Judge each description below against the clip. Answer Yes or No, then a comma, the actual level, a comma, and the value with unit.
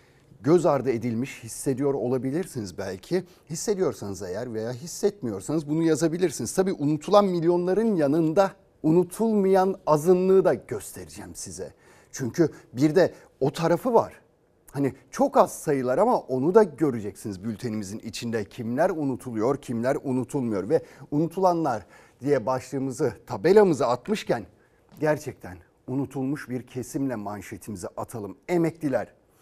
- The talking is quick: No, average, 110 wpm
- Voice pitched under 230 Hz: Yes, medium, 140 Hz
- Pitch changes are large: Yes, wide, 5.9 semitones